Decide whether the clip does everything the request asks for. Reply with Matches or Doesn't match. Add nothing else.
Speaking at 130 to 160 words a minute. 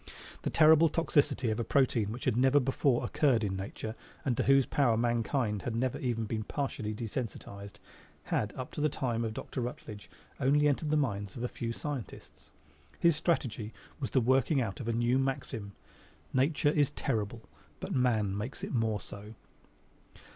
Doesn't match